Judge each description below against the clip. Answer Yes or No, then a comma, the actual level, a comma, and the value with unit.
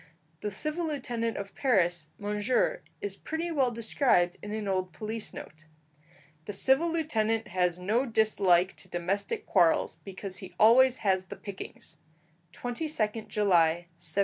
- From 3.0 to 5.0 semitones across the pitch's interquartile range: Yes, average, 4.6 semitones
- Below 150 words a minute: Yes, average, 140 wpm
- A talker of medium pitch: No, high, 210 Hz